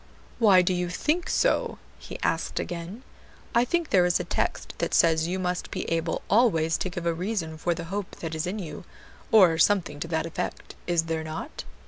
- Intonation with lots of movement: No, average, 3.1 semitones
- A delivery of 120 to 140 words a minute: No, average, 200 wpm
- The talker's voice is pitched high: No, medium, 175 Hz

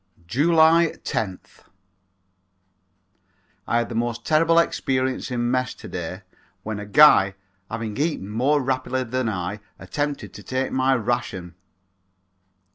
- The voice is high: No, low, 125 Hz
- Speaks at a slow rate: Yes, slow, 120 wpm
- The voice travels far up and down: No, average, 4.5 semitones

